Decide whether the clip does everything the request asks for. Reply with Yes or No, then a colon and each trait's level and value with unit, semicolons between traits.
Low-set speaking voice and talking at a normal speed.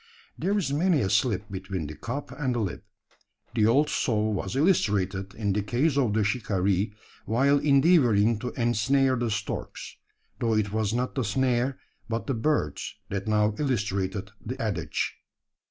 Yes: low, 110 Hz; average, 160 wpm